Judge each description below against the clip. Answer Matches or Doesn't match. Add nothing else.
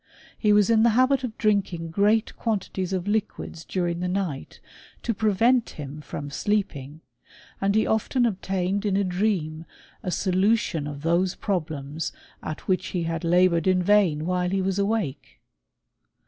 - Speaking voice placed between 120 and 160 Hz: Doesn't match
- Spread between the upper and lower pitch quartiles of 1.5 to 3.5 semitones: Doesn't match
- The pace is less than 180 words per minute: Matches